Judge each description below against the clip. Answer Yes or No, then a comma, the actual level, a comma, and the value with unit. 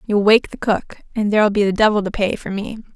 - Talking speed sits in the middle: No, fast, 265 wpm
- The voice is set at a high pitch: Yes, high, 205 Hz